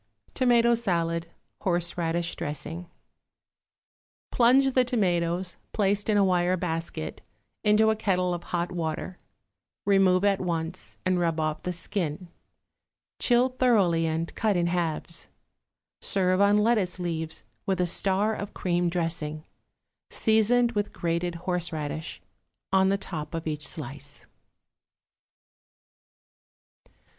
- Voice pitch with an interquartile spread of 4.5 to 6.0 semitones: No, average, 3.5 semitones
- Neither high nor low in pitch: Yes, medium, 180 Hz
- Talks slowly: Yes, slow, 115 wpm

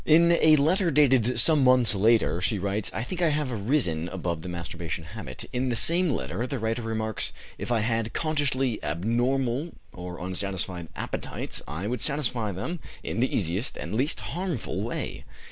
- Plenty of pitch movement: Yes, wide, 6.6 semitones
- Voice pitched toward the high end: No, low, 115 Hz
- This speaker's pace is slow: No, average, 170 wpm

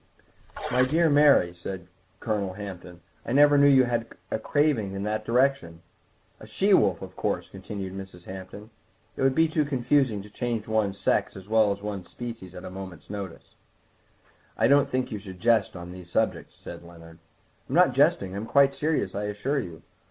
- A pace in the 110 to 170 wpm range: No, average, 185 wpm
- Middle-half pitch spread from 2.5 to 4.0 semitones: No, wide, 5.4 semitones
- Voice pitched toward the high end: No, low, 105 Hz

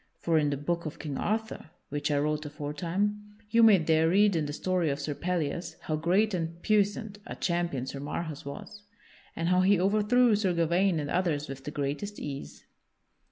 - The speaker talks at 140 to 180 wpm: No, average, 190 wpm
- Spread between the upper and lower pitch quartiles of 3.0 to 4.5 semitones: No, average, 5.2 semitones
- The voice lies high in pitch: No, medium, 170 Hz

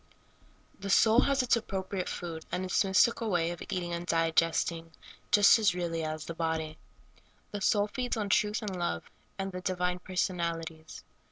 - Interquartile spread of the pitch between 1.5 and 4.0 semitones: Yes, average, 3.5 semitones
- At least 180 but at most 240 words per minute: No, average, 170 wpm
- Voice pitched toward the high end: No, medium, 180 Hz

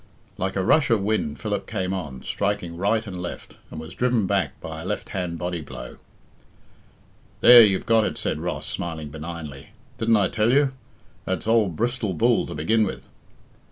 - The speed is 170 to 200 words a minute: Yes, average, 180 wpm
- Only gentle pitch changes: No, average, 4.8 semitones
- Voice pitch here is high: No, very low, 95 Hz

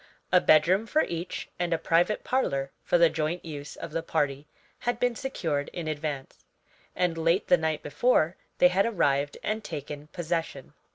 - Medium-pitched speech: Yes, medium, 165 Hz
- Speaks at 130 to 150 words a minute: No, average, 170 wpm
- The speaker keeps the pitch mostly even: No, average, 3.4 semitones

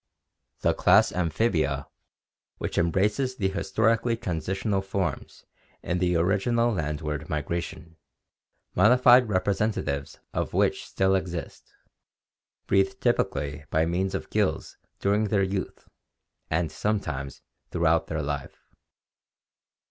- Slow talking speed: Yes, slow, 105 wpm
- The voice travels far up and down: No, average, 4.5 semitones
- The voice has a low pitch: Yes, very low, 95 Hz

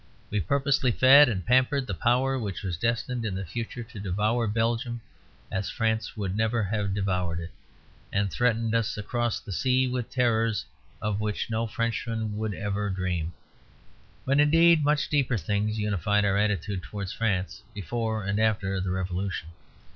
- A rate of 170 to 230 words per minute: No, average, 160 wpm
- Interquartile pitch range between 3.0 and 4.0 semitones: Yes, average, 3.3 semitones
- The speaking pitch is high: No, low, 110 Hz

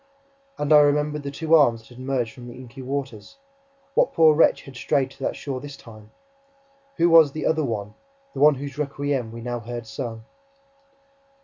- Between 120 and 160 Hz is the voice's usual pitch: Yes, low, 135 Hz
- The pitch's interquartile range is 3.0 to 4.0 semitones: Yes, average, 3.6 semitones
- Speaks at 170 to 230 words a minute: Yes, average, 190 wpm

